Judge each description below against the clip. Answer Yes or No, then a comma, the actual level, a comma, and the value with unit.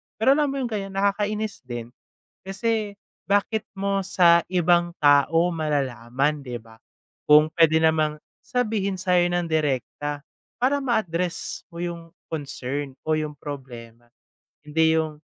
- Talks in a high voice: No, medium, 165 Hz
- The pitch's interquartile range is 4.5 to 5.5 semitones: Yes, average, 5.2 semitones